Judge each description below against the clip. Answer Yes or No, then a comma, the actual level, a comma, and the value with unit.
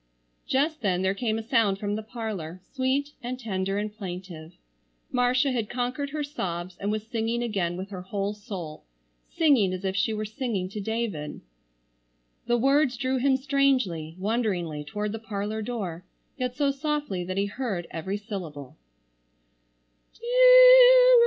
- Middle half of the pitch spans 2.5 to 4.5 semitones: No, average, 5.0 semitones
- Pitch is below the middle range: No, high, 215 Hz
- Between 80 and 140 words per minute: No, average, 150 wpm